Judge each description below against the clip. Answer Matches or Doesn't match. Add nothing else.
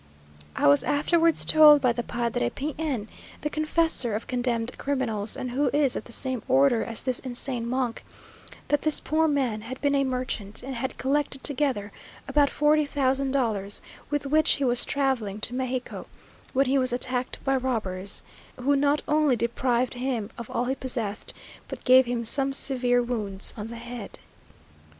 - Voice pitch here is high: Matches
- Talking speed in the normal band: Matches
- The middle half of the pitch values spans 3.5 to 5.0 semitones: Doesn't match